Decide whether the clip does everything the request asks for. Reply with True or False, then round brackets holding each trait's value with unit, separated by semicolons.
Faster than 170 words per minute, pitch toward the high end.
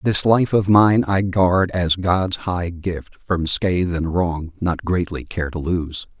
False (185 wpm; 90 Hz)